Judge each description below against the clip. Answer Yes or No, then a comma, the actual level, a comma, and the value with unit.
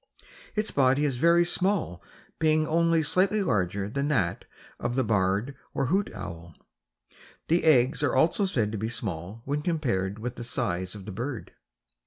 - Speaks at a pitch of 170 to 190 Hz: No, low, 130 Hz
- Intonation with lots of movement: Yes, wide, 7.6 semitones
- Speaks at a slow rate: No, average, 165 wpm